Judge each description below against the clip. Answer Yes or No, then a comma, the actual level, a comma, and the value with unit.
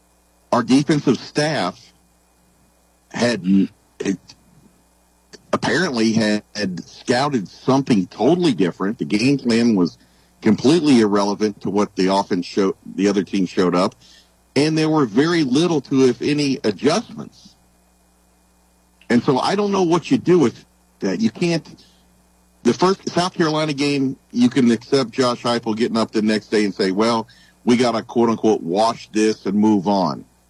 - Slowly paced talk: No, average, 150 wpm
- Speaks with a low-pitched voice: Yes, low, 110 Hz